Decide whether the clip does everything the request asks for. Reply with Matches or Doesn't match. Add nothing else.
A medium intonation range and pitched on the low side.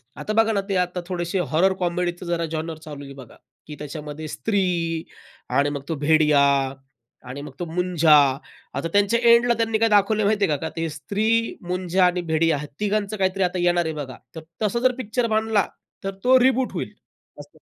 Doesn't match